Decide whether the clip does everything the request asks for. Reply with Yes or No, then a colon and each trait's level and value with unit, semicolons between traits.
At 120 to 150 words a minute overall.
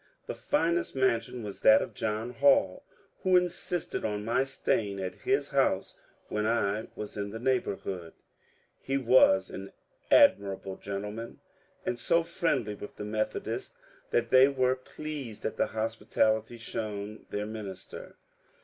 Yes: average, 140 wpm